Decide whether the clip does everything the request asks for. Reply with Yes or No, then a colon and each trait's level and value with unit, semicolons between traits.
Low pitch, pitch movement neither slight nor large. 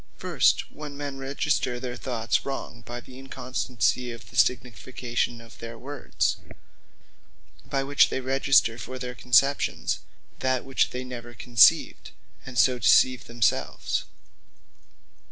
No: low, 125 Hz; narrow, 2.0 semitones